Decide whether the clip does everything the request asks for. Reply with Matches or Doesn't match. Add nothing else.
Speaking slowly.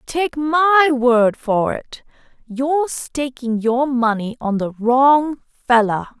Matches